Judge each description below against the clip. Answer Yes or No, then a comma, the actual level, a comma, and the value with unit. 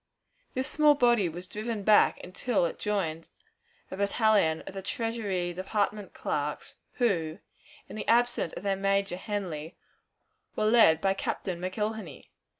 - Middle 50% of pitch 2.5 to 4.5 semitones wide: Yes, average, 3.6 semitones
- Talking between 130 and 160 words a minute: Yes, average, 140 wpm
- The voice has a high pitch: Yes, high, 195 Hz